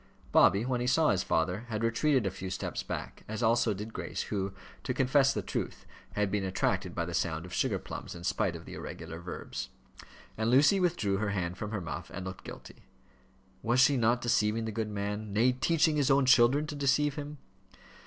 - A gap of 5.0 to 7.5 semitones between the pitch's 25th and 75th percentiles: Yes, average, 5.3 semitones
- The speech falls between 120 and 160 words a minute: No, fast, 205 wpm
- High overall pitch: No, low, 110 Hz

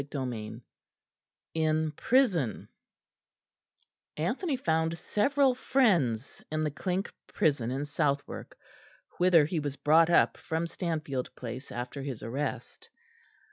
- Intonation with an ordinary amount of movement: Yes, average, 4.2 semitones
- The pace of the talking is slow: Yes, slow, 110 wpm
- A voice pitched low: No, medium, 155 Hz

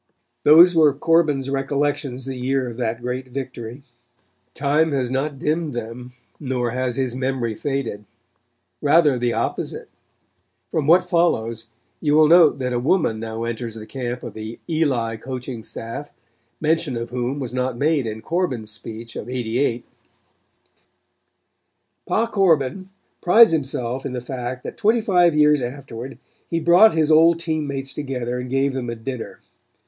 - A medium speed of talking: Yes, average, 155 wpm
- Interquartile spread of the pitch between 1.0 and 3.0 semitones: No, average, 4.1 semitones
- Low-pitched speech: Yes, low, 130 Hz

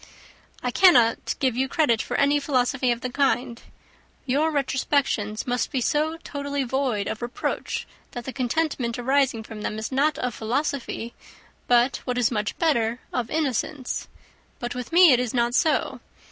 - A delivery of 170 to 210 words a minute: No, average, 160 wpm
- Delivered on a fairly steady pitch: No, average, 3.0 semitones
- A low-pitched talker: No, very high, 255 Hz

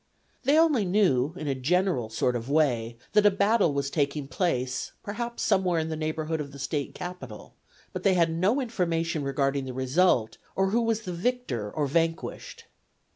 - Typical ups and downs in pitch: No, wide, 5.8 semitones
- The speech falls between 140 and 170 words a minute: No, average, 180 wpm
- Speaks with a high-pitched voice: No, medium, 165 Hz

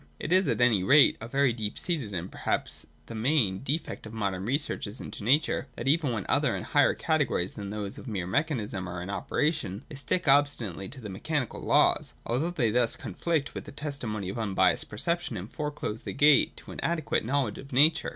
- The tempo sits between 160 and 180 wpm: No, fast, 205 wpm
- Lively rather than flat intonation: Yes, wide, 6.2 semitones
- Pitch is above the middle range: No, low, 120 Hz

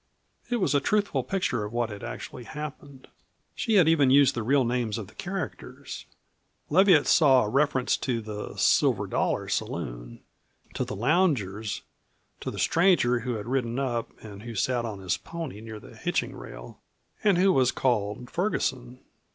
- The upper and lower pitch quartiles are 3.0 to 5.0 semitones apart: No, wide, 5.6 semitones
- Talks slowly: No, average, 165 wpm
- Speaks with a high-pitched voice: No, low, 125 Hz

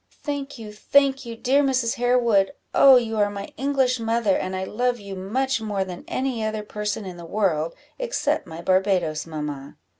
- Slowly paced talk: No, average, 180 wpm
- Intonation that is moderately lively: Yes, average, 5.0 semitones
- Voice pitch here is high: Yes, high, 215 Hz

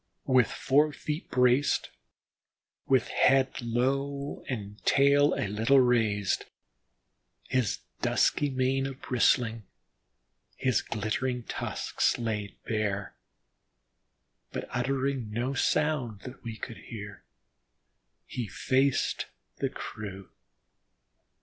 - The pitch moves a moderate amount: Yes, average, 3.7 semitones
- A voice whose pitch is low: Yes, low, 125 Hz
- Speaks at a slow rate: Yes, slow, 95 wpm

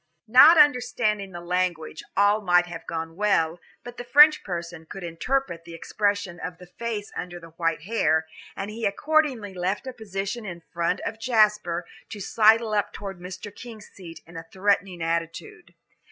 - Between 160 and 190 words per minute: Yes, average, 170 wpm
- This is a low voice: No, high, 195 Hz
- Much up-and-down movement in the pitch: No, average, 4.2 semitones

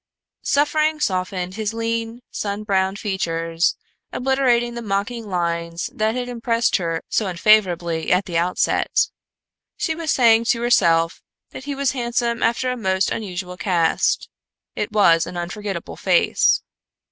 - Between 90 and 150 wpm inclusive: Yes, slow, 135 wpm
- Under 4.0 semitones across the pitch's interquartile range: No, average, 4.9 semitones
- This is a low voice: No, high, 210 Hz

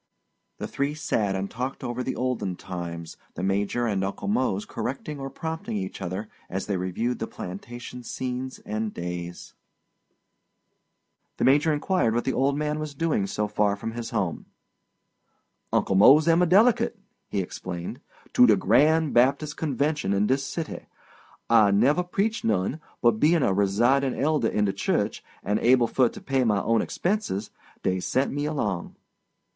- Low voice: Yes, low, 120 Hz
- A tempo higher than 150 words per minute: Yes, average, 160 wpm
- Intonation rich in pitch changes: Yes, wide, 6.4 semitones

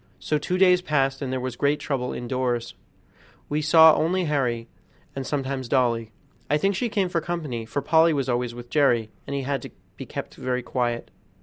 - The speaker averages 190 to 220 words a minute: Yes, average, 195 wpm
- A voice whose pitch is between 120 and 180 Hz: Yes, low, 135 Hz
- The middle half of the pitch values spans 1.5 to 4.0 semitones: Yes, average, 3.7 semitones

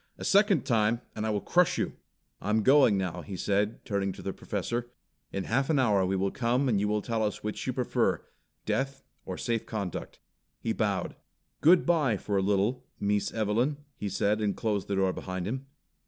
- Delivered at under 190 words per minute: No, average, 200 wpm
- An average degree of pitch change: Yes, average, 3.8 semitones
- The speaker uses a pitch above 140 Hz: No, low, 105 Hz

